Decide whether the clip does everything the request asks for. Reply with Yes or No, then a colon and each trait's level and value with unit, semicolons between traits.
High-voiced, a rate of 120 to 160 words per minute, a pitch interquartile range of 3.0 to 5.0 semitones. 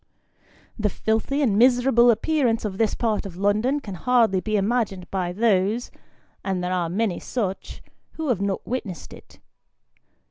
Yes: high, 215 Hz; average, 150 wpm; average, 4.1 semitones